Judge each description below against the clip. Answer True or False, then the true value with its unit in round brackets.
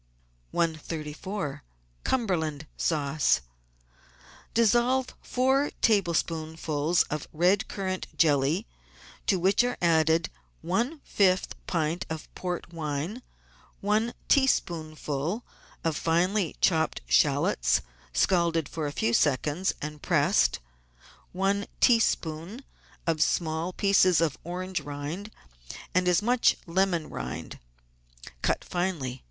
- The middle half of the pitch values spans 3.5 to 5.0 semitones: True (4.1 semitones)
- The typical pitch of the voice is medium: True (170 Hz)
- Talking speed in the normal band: False (100 wpm)